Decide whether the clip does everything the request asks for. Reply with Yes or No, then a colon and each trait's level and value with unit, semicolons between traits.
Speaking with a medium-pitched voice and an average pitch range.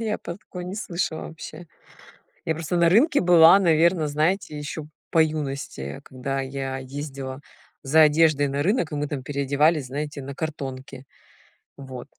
Yes: medium, 150 Hz; average, 3.4 semitones